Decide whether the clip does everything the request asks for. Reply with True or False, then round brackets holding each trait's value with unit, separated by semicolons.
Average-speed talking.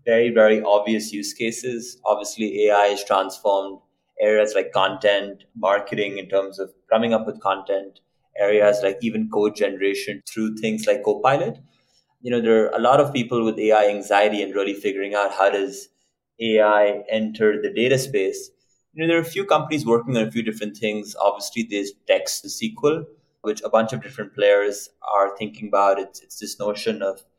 True (180 wpm)